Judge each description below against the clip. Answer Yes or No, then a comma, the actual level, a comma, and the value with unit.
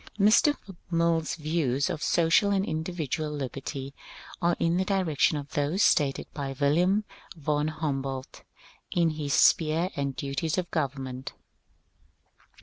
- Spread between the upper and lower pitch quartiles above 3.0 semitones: Yes, average, 3.4 semitones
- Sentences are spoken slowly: Yes, slow, 130 wpm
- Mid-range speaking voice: Yes, medium, 155 Hz